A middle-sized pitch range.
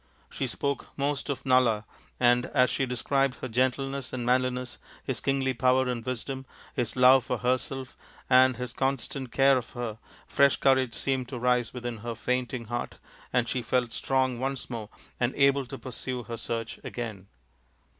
No: narrow, 1.7 semitones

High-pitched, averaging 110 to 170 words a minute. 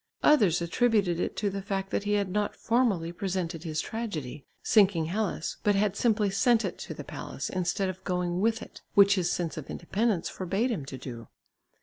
No: high, 195 Hz; average, 195 wpm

